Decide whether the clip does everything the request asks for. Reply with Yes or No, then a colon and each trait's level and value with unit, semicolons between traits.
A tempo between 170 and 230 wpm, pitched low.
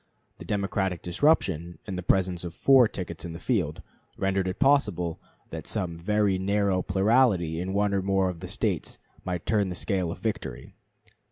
Yes: average, 175 wpm; very low, 95 Hz